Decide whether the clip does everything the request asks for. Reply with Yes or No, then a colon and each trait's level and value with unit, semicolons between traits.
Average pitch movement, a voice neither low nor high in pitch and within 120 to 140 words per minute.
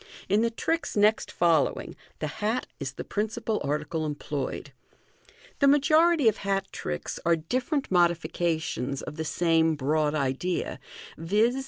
No: wide, 6.3 semitones; medium, 175 Hz; slow, 135 wpm